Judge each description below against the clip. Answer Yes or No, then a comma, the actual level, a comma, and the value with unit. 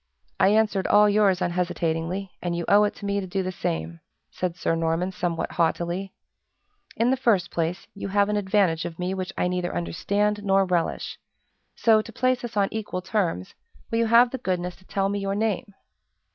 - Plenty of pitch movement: No, average, 2.9 semitones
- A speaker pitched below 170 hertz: No, high, 190 Hz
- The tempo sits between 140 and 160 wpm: No, average, 195 wpm